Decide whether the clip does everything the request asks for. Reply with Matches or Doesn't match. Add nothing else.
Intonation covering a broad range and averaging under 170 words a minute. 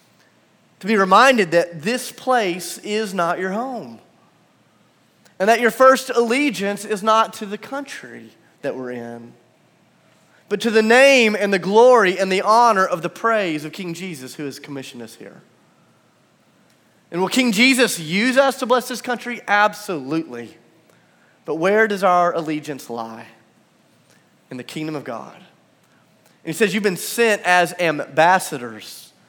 Matches